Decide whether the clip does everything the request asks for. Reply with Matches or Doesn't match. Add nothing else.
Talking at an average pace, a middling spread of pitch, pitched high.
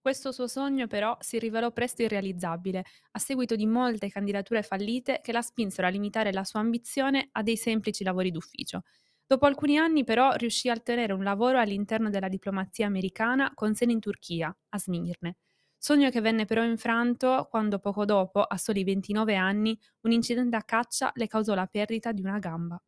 Doesn't match